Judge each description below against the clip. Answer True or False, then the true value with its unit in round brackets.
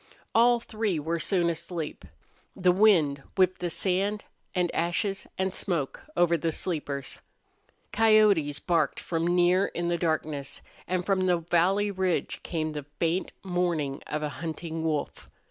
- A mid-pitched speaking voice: True (175 Hz)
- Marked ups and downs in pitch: False (3.0 semitones)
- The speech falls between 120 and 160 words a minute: True (140 wpm)